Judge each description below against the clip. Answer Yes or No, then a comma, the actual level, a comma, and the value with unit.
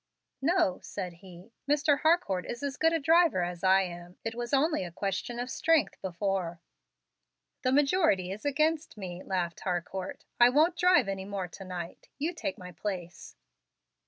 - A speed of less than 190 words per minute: Yes, average, 165 wpm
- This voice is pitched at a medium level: No, high, 205 Hz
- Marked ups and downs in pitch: Yes, wide, 8.4 semitones